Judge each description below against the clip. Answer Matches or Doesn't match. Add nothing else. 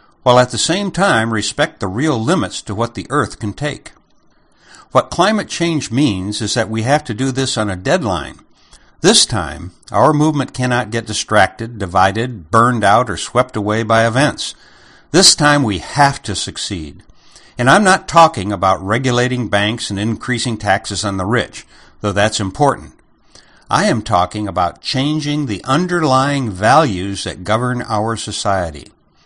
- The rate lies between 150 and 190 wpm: Matches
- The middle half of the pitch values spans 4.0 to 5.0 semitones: Matches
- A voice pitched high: Doesn't match